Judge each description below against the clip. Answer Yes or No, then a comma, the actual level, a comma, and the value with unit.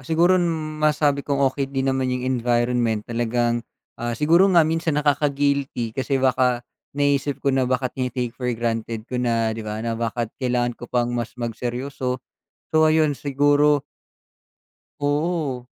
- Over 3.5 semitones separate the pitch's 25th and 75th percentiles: No, average, 3.1 semitones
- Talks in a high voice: No, low, 130 Hz